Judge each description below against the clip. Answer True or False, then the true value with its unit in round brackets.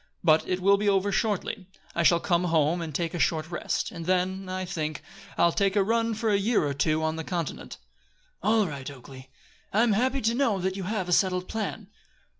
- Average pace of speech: False (220 wpm)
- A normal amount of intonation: True (3.9 semitones)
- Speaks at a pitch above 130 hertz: True (185 Hz)